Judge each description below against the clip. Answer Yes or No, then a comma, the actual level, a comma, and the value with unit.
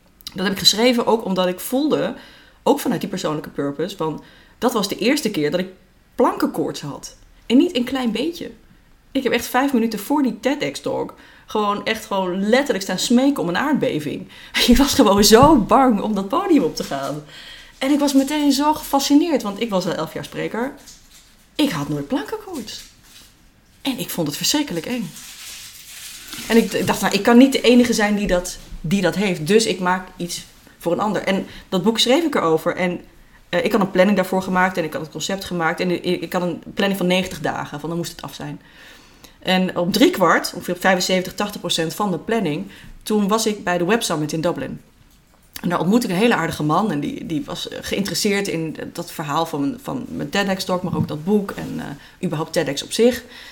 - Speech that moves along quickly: Yes, fast, 205 wpm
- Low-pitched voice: No, high, 195 Hz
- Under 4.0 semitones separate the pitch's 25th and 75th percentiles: No, wide, 5.6 semitones